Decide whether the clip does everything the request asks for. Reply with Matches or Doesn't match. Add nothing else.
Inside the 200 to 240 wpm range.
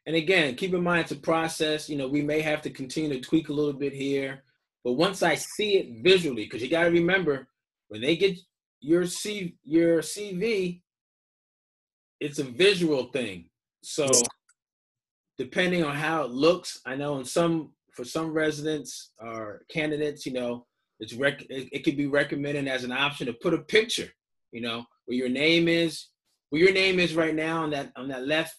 Doesn't match